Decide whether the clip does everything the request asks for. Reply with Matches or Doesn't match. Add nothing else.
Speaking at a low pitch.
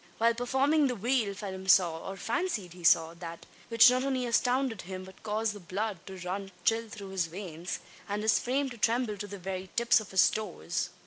Doesn't match